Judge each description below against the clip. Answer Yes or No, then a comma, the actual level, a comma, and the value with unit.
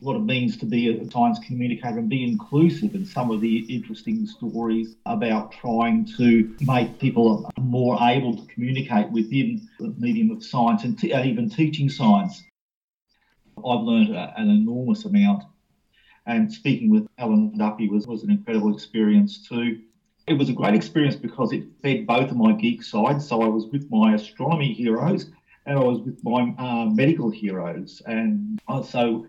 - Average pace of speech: Yes, average, 170 wpm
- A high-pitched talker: No, low, 135 Hz